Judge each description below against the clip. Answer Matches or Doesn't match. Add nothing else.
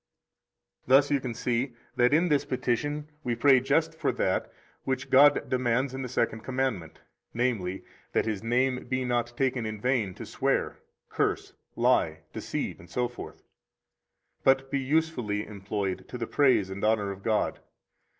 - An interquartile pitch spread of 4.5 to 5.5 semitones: Doesn't match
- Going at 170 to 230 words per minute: Doesn't match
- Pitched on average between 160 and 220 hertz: Doesn't match